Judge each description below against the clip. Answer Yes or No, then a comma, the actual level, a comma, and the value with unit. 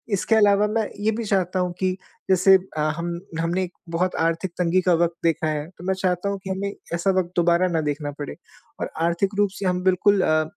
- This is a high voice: No, medium, 180 Hz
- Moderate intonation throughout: No, narrow, 2.2 semitones